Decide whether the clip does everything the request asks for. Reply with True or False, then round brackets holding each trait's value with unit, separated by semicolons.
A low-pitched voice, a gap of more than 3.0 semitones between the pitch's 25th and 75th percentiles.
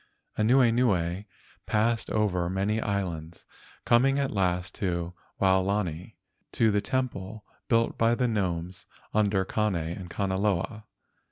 True (100 Hz; 3.5 semitones)